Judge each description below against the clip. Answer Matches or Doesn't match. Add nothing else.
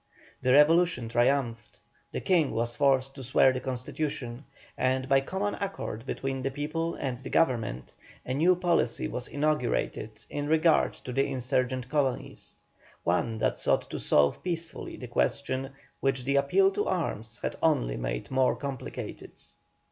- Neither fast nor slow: Matches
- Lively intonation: Doesn't match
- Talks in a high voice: Doesn't match